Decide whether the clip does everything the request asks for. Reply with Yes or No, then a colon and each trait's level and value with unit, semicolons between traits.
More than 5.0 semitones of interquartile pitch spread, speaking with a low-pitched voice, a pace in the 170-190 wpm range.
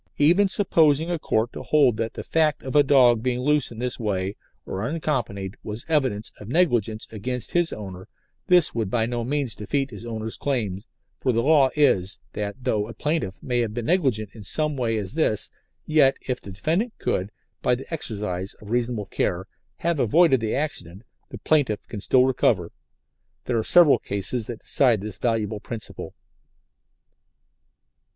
Yes: wide, 5.5 semitones; low, 120 Hz; average, 175 wpm